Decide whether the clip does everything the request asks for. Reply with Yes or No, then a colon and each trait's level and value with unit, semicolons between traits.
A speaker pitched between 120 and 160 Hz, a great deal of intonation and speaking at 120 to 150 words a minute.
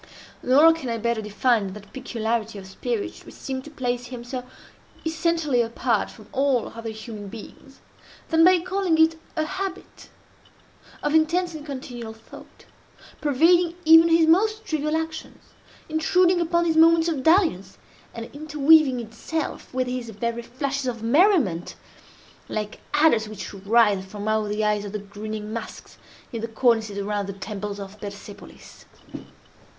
No: very high, 250 Hz; wide, 6.8 semitones; average, 145 wpm